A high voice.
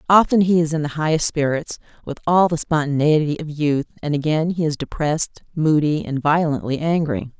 No: medium, 155 Hz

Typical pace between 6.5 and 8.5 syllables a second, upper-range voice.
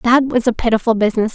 Yes: 6.9 syllables/s; high, 230 Hz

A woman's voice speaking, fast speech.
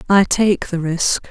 No: female; average, 185 wpm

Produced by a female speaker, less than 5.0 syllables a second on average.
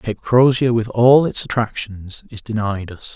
No: male; 4.3 syllables/s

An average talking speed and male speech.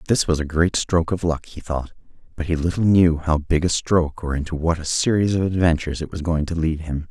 No: fast, 255 wpm; male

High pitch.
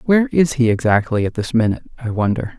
No: low, 125 Hz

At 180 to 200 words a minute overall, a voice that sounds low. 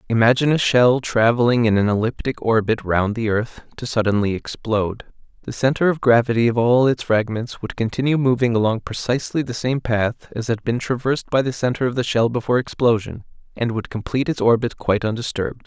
Yes: average, 190 wpm; low, 120 Hz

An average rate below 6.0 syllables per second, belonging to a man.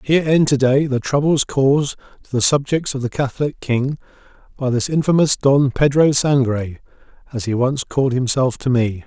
Yes: 5.2 syllables/s; male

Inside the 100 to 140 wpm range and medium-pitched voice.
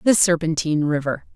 Yes: slow, 135 wpm; medium, 165 Hz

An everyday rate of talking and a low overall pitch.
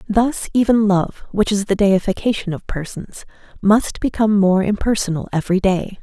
No: average, 150 wpm; high, 200 Hz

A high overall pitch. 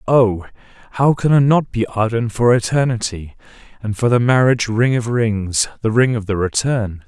No: low, 115 Hz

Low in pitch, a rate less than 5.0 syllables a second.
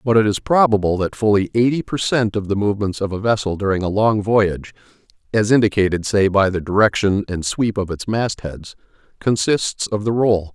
No: low, 105 Hz; 5.3 syllables/s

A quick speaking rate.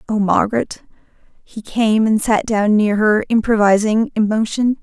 No: slow, 135 wpm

